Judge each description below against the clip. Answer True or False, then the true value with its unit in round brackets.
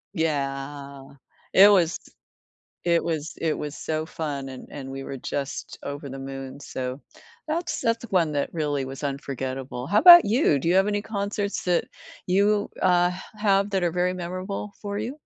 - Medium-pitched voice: True (165 Hz)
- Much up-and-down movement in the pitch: True (6.3 semitones)